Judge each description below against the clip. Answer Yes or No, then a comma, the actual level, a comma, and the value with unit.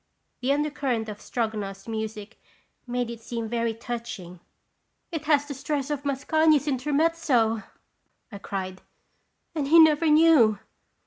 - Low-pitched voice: No, very high, 250 Hz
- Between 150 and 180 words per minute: No, slow, 135 wpm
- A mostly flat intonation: No, average, 5.1 semitones